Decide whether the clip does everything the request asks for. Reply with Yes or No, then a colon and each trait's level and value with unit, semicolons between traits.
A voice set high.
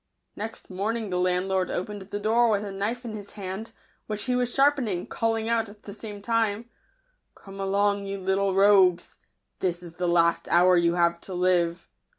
Yes: high, 200 Hz